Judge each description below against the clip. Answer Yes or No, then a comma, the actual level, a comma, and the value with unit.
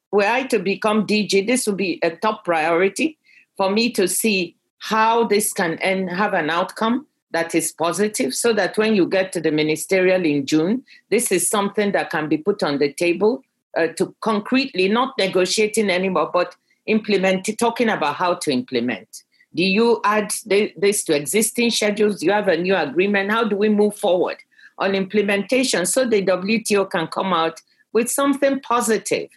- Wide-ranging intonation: No, average, 3.6 semitones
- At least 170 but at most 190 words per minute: Yes, average, 180 wpm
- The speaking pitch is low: No, high, 205 Hz